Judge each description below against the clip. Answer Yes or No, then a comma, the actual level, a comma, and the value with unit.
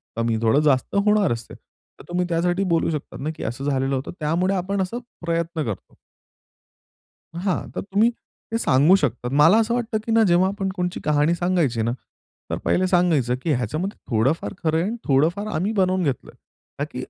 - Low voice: No, medium, 170 Hz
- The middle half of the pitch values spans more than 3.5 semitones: Yes, wide, 5.6 semitones